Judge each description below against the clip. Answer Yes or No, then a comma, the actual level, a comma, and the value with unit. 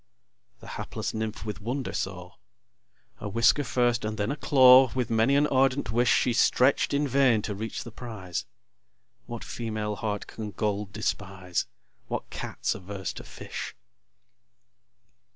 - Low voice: Yes, low, 110 Hz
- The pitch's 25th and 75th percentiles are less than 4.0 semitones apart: Yes, average, 3.6 semitones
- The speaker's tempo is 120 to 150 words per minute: Yes, average, 145 wpm